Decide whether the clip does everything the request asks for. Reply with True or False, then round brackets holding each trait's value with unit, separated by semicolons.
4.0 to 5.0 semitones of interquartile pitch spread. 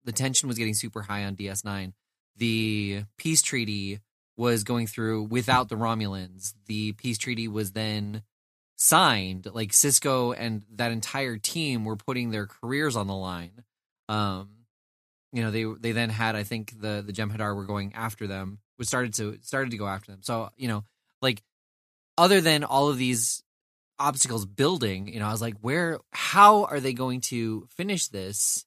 False (3.3 semitones)